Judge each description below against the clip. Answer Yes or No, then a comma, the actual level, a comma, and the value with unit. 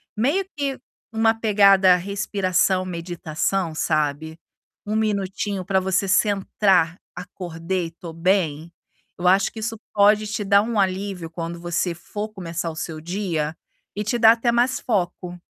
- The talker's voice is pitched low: No, high, 190 Hz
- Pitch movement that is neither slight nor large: Yes, average, 3.5 semitones